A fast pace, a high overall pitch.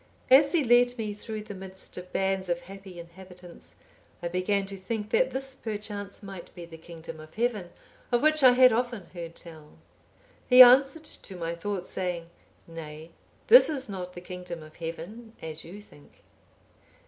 No: average, 170 wpm; high, 195 Hz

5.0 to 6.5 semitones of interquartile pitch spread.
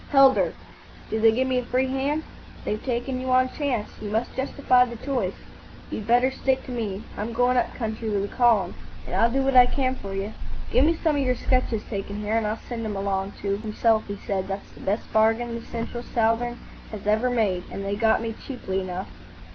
No: average, 3.4 semitones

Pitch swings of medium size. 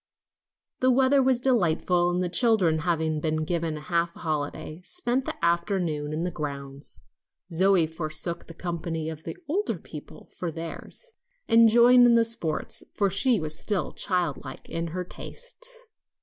No: wide, 6.5 semitones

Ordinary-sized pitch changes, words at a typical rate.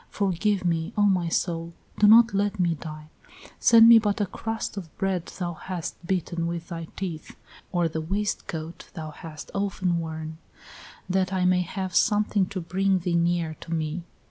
Yes: average, 3.1 semitones; average, 170 wpm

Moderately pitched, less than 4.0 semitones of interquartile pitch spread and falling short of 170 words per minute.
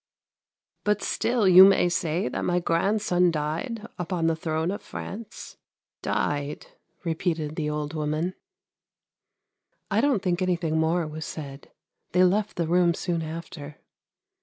Yes: medium, 170 Hz; average, 2.8 semitones; average, 145 wpm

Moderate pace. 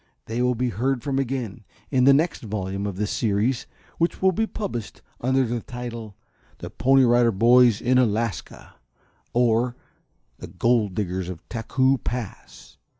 Yes: average, 150 wpm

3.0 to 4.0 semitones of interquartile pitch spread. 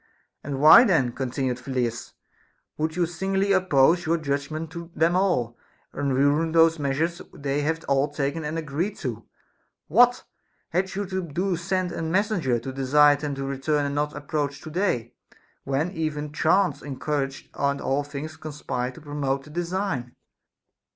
Yes: average, 3.6 semitones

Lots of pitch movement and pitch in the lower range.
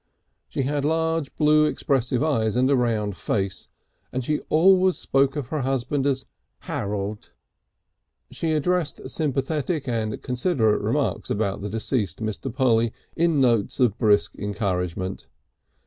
Yes: wide, 5.7 semitones; low, 130 Hz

